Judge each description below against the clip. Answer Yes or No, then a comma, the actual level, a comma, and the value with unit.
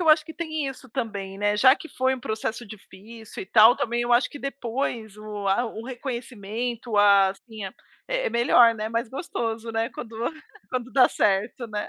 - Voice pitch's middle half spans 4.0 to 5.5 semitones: No, average, 3.3 semitones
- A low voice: No, high, 230 Hz